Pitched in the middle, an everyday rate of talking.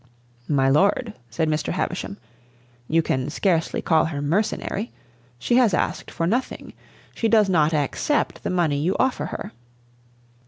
Yes: medium, 170 Hz; average, 145 wpm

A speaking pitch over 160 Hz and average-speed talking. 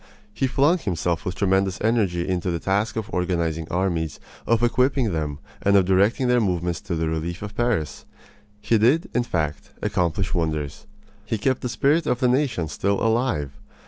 No: very low, 95 Hz; average, 175 wpm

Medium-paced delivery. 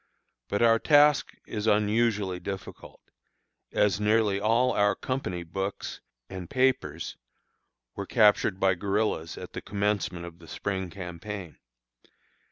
No: slow, 120 wpm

